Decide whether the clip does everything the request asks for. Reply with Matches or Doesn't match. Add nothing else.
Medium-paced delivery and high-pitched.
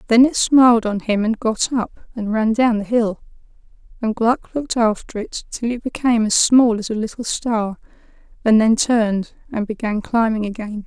Matches